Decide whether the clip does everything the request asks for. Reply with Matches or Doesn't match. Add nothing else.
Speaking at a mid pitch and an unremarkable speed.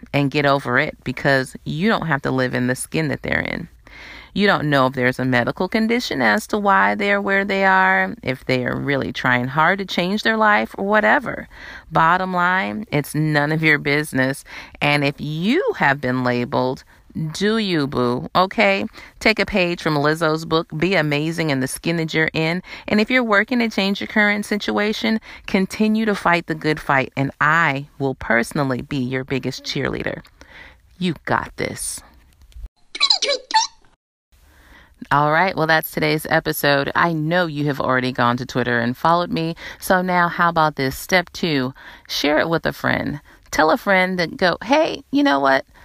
Matches